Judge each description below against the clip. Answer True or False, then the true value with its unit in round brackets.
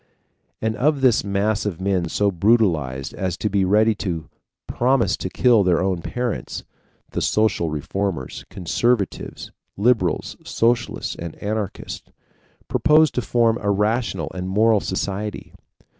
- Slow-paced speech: True (130 wpm)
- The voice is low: True (100 Hz)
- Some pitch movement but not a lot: True (3.7 semitones)